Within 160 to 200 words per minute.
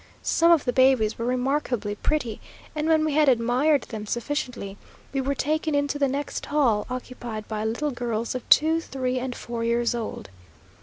Yes: average, 175 wpm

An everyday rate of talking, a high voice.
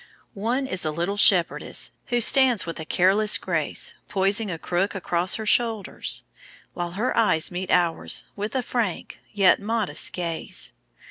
Yes: average, 145 wpm; high, 195 Hz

